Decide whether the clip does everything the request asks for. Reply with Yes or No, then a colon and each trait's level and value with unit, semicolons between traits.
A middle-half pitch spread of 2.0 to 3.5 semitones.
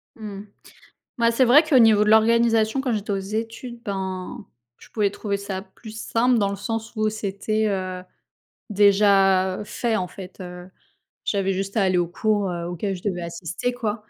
Yes: average, 2.9 semitones